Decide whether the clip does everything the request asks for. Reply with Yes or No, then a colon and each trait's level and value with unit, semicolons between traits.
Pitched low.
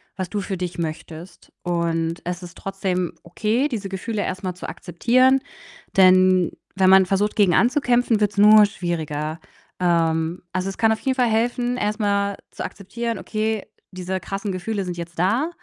No: high, 195 Hz